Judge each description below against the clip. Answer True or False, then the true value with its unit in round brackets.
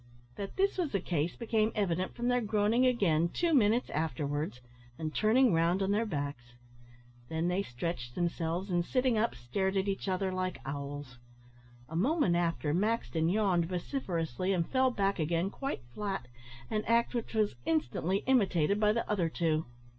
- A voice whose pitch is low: False (185 Hz)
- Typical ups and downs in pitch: True (5.0 semitones)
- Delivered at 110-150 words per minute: False (165 wpm)